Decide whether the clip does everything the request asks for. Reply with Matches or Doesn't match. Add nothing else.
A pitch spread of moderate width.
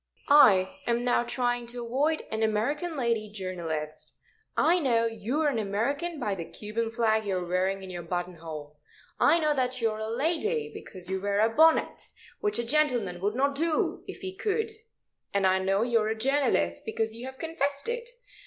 Doesn't match